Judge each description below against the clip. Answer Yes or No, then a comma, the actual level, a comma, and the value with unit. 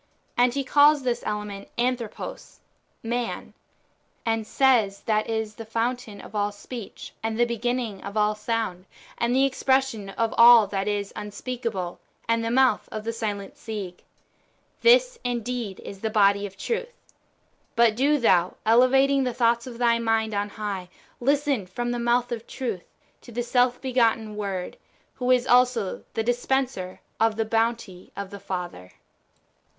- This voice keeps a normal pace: Yes, average, 155 wpm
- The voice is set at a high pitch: Yes, high, 230 Hz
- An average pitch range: Yes, average, 3.1 semitones